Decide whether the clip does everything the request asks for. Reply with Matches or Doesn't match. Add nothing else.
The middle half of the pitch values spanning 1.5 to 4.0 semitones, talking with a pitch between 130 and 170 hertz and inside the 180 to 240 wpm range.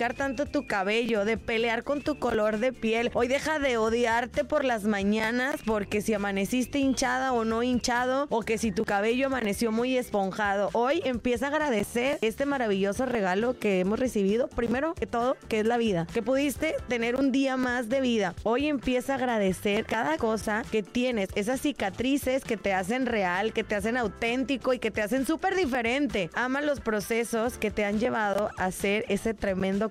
Doesn't match